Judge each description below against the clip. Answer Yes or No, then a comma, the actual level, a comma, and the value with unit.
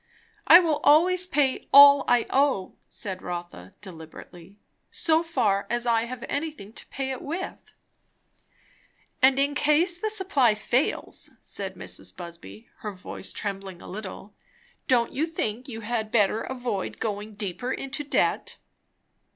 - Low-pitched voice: No, high, 240 Hz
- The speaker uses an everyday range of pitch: No, wide, 6.3 semitones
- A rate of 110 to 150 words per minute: Yes, average, 140 wpm